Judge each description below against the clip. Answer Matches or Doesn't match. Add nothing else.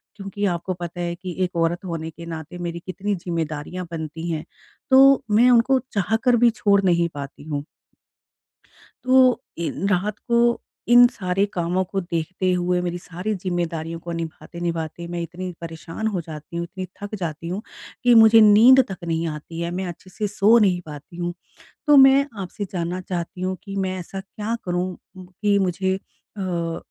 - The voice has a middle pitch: Matches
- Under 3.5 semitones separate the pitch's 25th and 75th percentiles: Matches